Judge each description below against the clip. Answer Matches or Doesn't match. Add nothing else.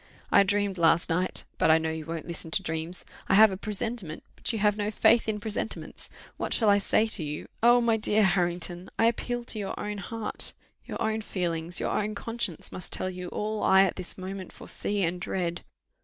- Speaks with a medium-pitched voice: Doesn't match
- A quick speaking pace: Matches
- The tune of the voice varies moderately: Matches